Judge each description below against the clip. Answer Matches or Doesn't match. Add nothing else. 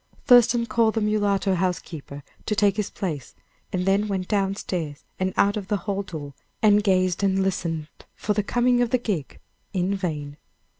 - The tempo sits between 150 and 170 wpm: Doesn't match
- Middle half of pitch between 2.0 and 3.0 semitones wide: Matches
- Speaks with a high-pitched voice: Matches